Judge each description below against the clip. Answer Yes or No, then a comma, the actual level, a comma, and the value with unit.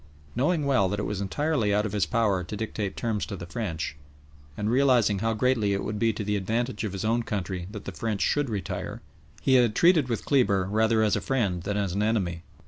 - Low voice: Yes, low, 105 Hz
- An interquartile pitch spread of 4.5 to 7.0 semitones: No, average, 3.1 semitones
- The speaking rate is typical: No, fast, 225 wpm